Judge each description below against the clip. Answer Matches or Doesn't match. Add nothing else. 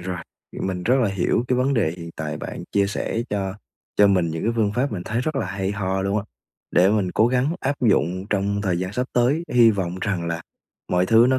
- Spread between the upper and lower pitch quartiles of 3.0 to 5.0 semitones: Matches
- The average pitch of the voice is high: Doesn't match